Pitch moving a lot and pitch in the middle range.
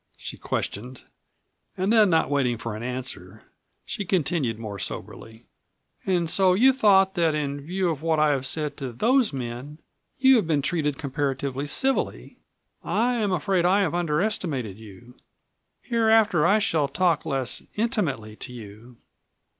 Yes: wide, 7.2 semitones; medium, 150 Hz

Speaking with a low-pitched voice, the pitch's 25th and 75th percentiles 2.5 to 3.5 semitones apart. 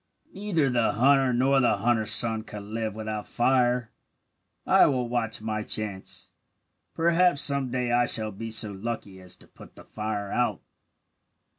Yes: low, 120 Hz; average, 3.1 semitones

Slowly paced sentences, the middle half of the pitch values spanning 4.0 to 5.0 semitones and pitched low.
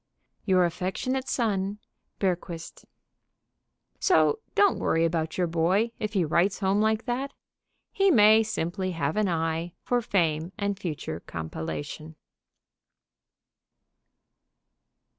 No: slow, 105 wpm; average, 4.7 semitones; medium, 185 Hz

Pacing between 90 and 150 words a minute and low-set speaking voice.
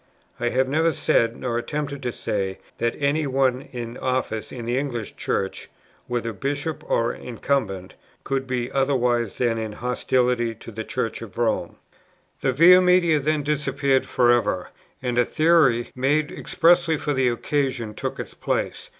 No: average, 160 wpm; low, 125 Hz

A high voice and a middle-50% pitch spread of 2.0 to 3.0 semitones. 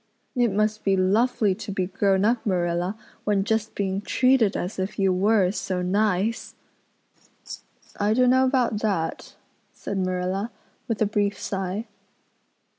Yes: high, 200 Hz; average, 2.7 semitones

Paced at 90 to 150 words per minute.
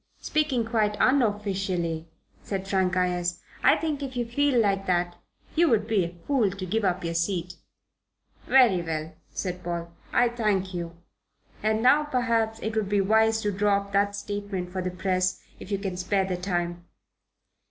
No: average, 175 wpm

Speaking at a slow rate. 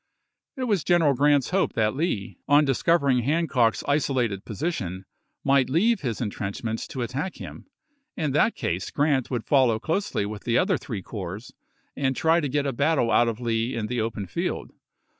No: average, 180 wpm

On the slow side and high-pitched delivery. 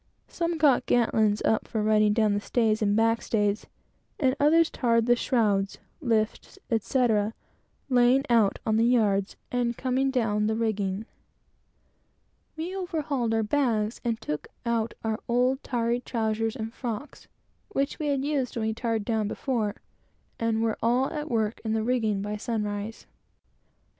No: average, 155 wpm; high, 230 Hz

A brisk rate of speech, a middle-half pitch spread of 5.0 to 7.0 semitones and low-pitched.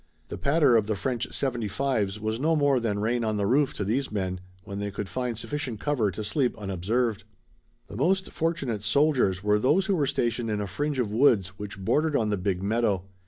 Yes: fast, 210 wpm; average, 5.3 semitones; low, 115 Hz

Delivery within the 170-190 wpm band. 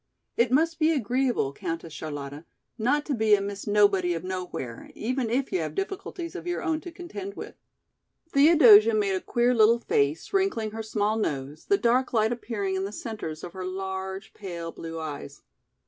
Yes: average, 180 wpm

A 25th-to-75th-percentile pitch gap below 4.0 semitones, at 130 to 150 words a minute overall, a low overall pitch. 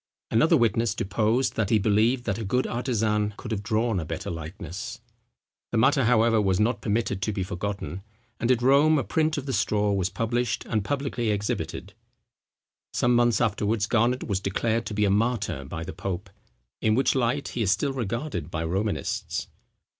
No: average, 3.3 semitones; average, 180 wpm; low, 110 Hz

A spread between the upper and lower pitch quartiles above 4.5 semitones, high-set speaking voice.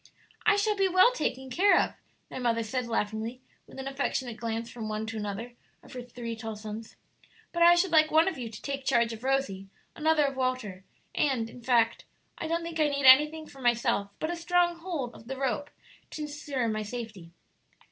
Yes: wide, 5.4 semitones; very high, 255 Hz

